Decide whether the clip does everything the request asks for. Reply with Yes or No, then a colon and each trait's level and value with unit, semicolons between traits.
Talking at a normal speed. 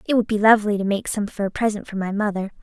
No: fast, 295 wpm